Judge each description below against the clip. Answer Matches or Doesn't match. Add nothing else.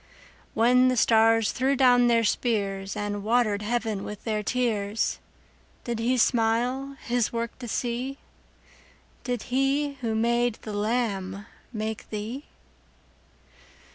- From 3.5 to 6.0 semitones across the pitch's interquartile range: Doesn't match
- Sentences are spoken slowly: Matches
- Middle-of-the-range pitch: Doesn't match